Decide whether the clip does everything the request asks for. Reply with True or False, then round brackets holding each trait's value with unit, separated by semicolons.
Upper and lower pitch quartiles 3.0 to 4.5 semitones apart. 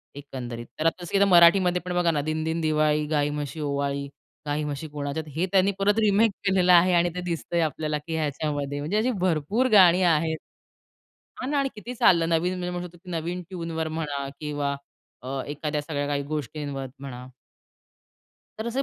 True (3.6 semitones)